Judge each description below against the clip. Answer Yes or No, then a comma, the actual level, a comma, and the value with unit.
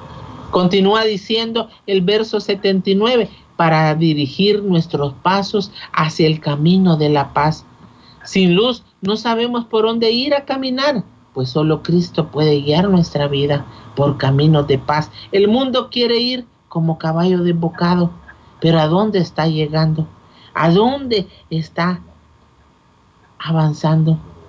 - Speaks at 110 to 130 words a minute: Yes, slow, 125 wpm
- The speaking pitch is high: No, medium, 165 Hz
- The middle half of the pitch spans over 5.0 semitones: Yes, wide, 5.6 semitones